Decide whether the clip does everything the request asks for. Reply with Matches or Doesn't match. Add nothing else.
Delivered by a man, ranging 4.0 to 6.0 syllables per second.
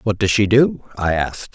Matches